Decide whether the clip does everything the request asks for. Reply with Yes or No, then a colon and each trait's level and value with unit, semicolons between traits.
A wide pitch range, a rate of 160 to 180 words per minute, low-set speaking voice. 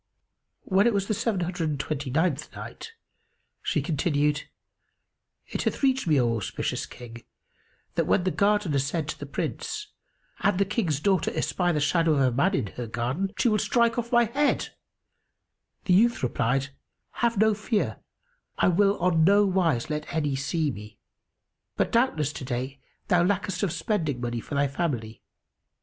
No: wide, 6.6 semitones; average, 170 wpm; medium, 165 Hz